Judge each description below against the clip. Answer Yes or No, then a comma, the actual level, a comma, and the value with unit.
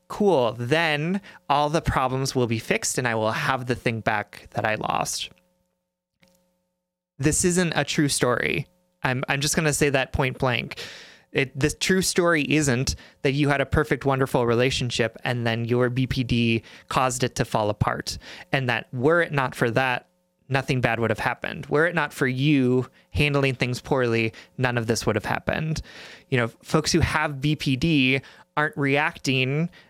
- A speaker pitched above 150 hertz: No, medium, 140 Hz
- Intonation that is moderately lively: Yes, average, 3.9 semitones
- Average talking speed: Yes, average, 175 wpm